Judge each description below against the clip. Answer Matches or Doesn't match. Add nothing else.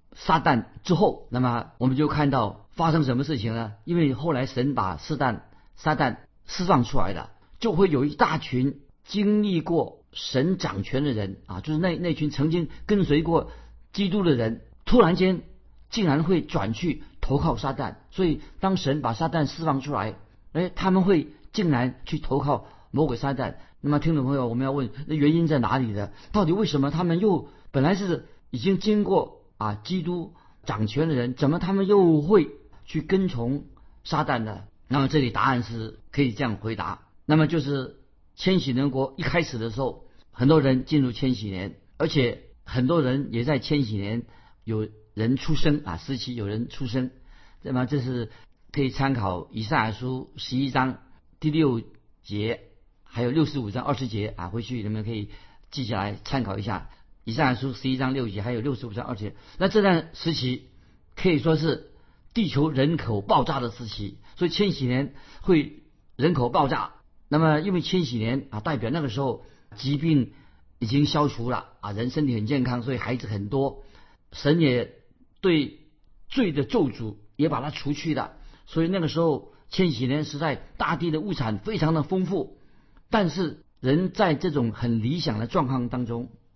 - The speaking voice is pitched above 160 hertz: Doesn't match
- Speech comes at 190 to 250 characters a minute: Doesn't match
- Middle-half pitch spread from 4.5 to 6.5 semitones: Matches